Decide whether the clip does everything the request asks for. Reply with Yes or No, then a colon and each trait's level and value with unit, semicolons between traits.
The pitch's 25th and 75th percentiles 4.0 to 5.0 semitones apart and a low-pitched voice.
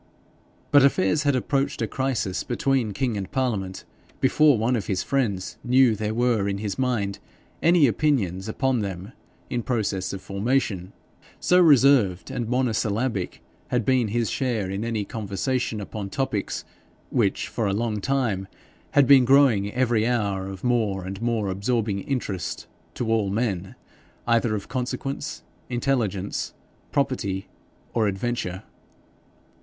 Yes: average, 4.5 semitones; low, 115 Hz